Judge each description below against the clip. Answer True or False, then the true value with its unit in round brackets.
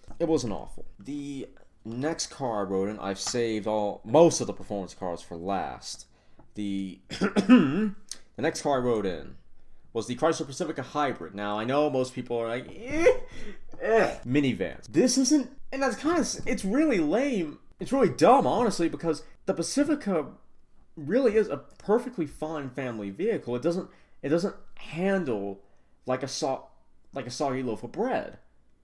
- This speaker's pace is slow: False (160 wpm)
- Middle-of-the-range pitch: True (145 Hz)